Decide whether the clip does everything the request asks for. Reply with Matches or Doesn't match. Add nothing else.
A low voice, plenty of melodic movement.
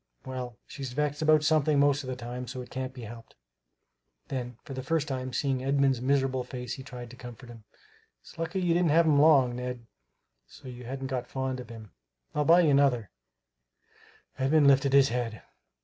Doesn't match